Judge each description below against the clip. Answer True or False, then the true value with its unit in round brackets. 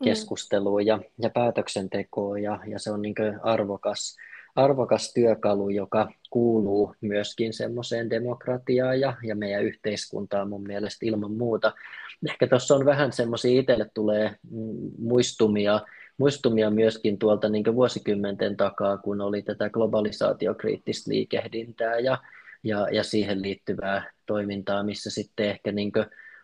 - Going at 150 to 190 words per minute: False (125 wpm)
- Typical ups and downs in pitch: False (2.2 semitones)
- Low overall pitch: True (110 Hz)